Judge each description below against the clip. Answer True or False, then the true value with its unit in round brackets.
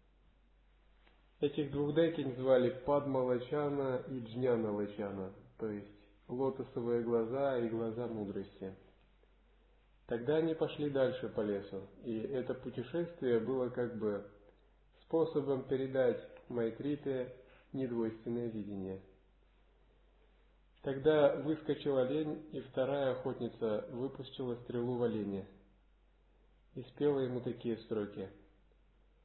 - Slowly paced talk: True (95 wpm)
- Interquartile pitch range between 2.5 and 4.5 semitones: True (4.1 semitones)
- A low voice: True (125 Hz)